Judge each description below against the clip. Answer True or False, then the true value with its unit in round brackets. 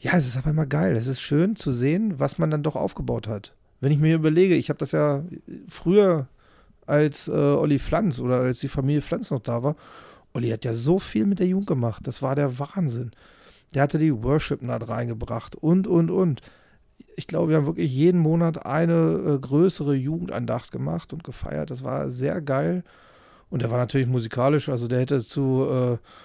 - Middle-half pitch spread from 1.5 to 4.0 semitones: False (4.4 semitones)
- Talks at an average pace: False (195 wpm)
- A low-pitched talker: False (145 Hz)